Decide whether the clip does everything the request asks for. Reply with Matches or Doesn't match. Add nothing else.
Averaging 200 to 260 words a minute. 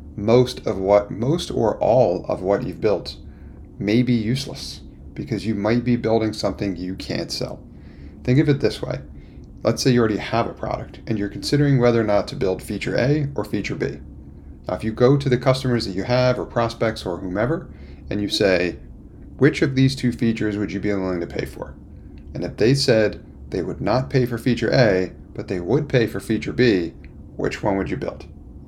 Matches